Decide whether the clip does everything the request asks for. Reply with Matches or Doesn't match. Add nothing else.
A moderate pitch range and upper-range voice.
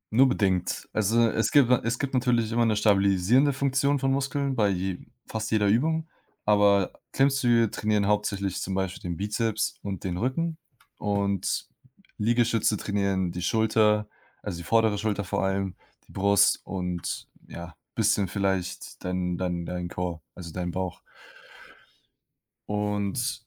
Doesn't match